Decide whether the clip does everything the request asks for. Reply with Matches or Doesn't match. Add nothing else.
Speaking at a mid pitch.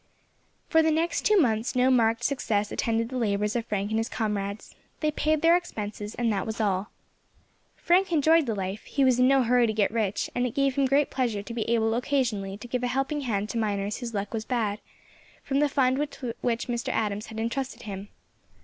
Doesn't match